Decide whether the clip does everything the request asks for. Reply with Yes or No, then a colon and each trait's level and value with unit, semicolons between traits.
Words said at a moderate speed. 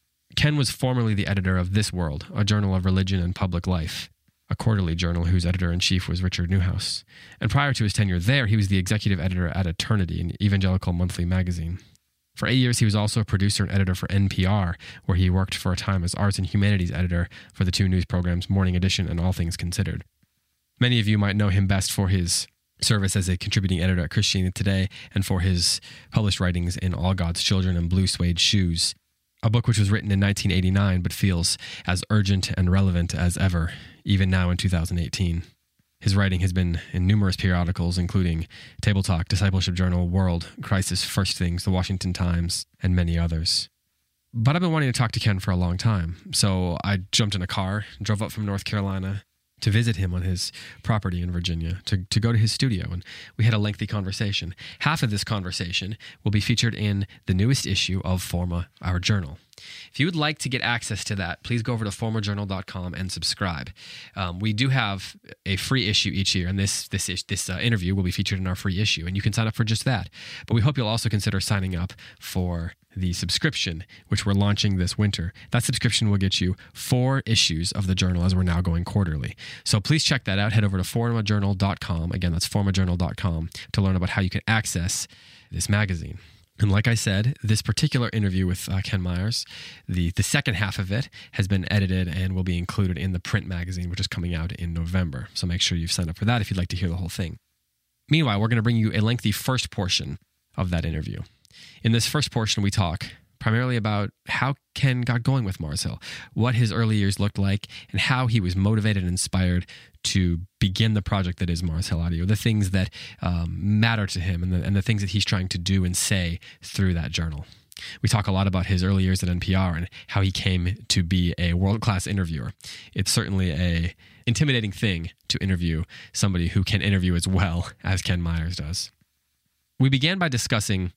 No: fast, 215 wpm